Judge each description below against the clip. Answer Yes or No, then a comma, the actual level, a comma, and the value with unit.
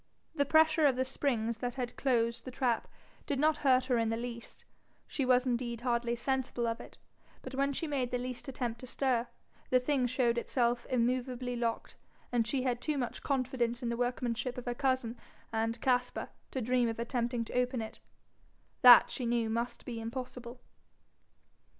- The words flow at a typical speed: Yes, average, 180 wpm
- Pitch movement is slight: Yes, narrow, 1.6 semitones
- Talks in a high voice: Yes, high, 245 Hz